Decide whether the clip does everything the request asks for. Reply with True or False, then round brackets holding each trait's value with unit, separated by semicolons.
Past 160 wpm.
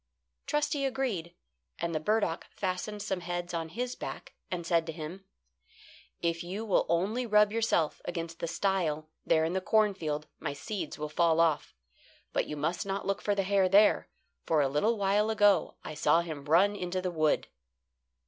True (175 wpm)